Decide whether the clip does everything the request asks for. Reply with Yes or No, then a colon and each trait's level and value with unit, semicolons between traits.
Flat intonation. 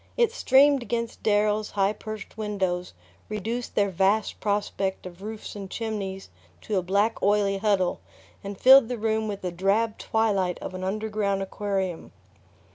Yes: narrow, 2.2 semitones